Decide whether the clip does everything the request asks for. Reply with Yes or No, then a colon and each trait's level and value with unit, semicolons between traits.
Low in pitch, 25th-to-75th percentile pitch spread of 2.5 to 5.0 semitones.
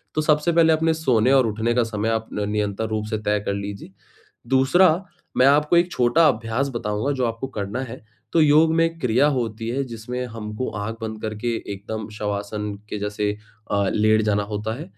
Yes: low, 115 Hz; average, 4.2 semitones